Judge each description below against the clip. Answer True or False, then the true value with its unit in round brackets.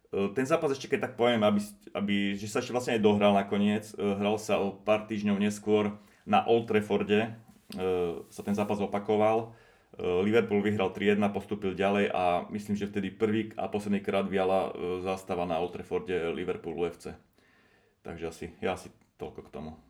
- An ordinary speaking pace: False (170 wpm)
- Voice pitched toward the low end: True (105 Hz)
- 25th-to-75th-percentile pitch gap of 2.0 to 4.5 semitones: False (1.3 semitones)